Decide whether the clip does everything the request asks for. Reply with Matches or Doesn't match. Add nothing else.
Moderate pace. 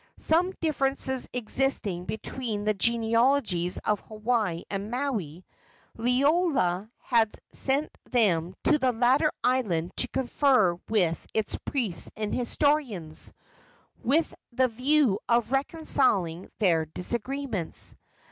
Doesn't match